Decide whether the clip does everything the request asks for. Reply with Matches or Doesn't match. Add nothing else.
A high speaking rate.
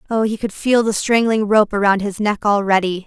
Matches